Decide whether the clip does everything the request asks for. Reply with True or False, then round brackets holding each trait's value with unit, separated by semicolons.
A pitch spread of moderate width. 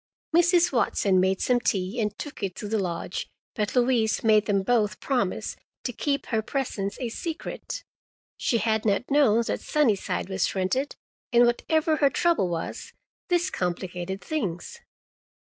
False (6.0 semitones)